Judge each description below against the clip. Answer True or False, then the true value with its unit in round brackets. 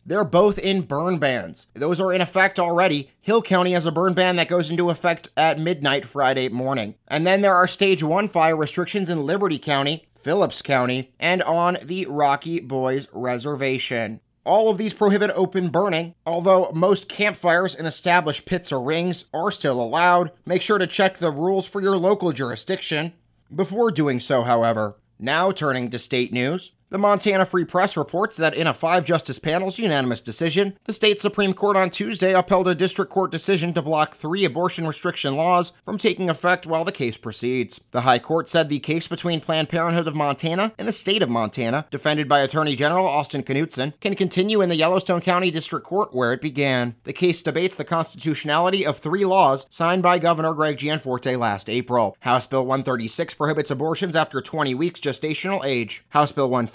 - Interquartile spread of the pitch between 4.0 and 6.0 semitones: True (4.7 semitones)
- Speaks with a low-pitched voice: False (165 Hz)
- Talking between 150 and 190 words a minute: True (185 wpm)